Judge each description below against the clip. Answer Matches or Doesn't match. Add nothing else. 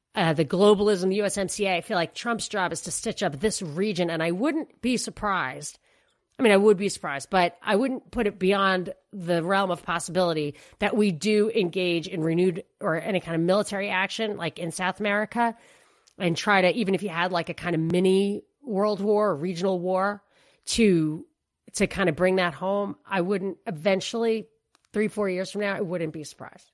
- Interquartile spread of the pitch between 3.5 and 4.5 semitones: Doesn't match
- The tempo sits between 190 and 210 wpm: Matches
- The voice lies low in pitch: Doesn't match